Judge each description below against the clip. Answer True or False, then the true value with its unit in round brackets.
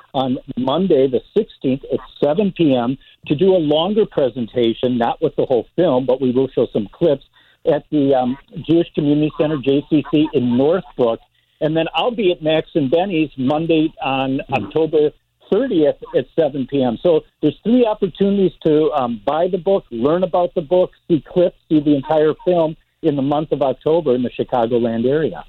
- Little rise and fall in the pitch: False (4.3 semitones)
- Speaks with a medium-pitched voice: True (155 Hz)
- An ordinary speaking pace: True (175 wpm)